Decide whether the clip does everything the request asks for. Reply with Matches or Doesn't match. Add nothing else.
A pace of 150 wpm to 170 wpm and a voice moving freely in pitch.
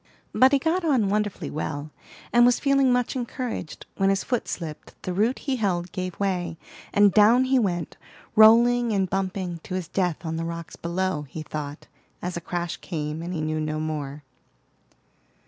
Doesn't match